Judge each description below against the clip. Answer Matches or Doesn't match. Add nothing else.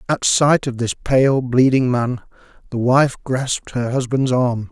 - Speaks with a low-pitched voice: Matches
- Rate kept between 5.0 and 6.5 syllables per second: Doesn't match